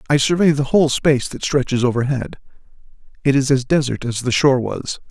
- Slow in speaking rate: No, average, 190 wpm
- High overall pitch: No, low, 135 Hz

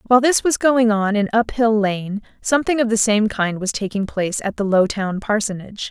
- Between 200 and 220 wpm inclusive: Yes, fast, 205 wpm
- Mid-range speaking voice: No, high, 215 Hz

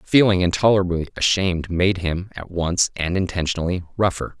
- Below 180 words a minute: Yes, slow, 135 wpm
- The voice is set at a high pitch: No, very low, 90 Hz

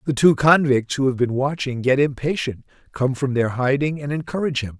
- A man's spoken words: Yes, male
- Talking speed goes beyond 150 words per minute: Yes, average, 200 wpm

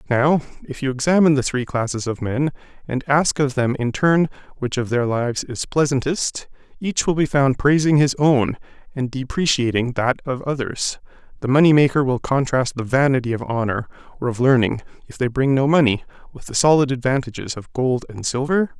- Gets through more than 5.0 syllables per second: Yes, 5.3 syllables/s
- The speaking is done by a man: Yes, male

